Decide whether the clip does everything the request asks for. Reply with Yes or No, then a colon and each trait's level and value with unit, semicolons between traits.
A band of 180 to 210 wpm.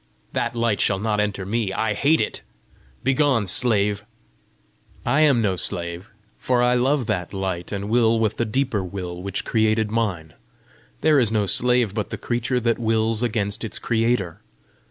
No: average, 165 wpm